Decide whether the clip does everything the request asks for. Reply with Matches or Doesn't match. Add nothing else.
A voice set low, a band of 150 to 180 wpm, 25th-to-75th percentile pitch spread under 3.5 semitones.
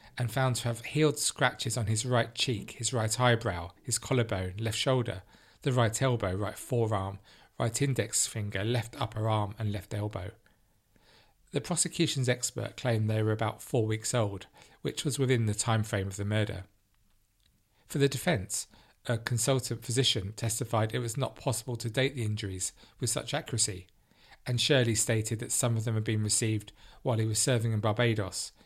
Matches